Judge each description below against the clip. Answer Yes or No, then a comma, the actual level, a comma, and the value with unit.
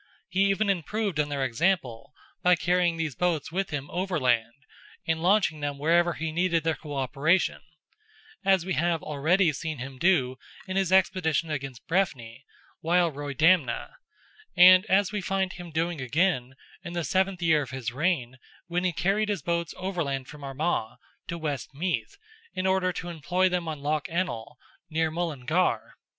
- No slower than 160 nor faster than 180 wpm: Yes, average, 165 wpm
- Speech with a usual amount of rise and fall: Yes, average, 4.3 semitones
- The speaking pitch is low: No, medium, 165 Hz